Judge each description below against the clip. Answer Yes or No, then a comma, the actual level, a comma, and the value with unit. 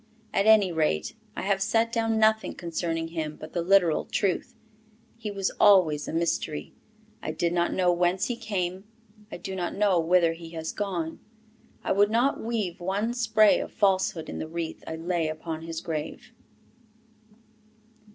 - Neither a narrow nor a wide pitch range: Yes, average, 3.9 semitones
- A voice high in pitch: No, medium, 180 Hz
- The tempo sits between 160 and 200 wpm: Yes, average, 165 wpm